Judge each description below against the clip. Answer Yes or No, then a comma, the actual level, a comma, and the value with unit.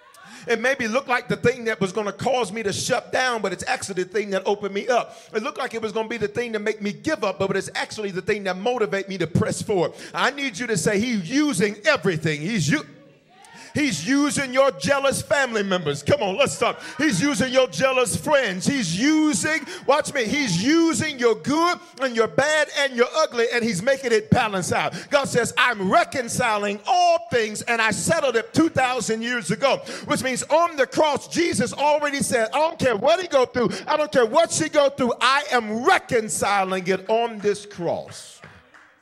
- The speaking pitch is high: Yes, high, 240 Hz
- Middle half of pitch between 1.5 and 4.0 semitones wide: No, average, 5.3 semitones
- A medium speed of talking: No, fast, 210 wpm